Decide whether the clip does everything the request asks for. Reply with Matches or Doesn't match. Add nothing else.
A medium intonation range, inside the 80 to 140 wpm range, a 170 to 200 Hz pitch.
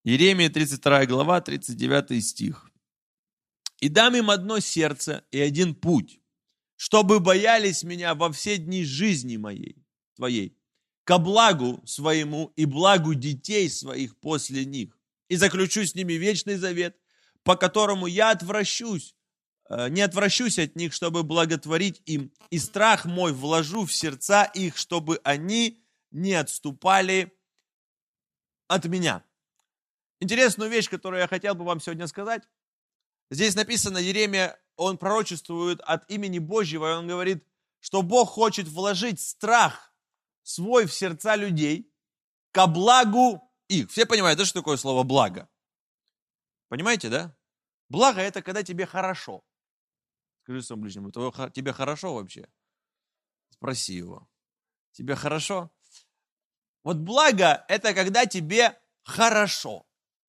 Matches